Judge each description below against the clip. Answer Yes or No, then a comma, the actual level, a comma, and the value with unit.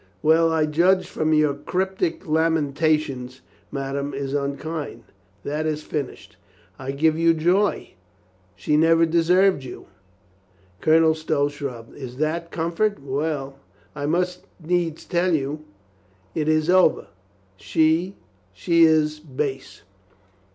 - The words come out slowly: Yes, slow, 120 wpm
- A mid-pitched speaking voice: Yes, medium, 155 Hz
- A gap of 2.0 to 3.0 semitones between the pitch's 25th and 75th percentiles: Yes, average, 2.7 semitones